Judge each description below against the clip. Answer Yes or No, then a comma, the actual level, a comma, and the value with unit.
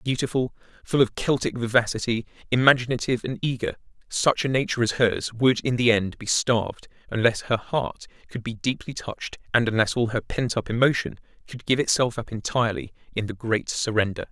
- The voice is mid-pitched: No, low, 120 Hz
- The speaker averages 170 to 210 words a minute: Yes, average, 175 wpm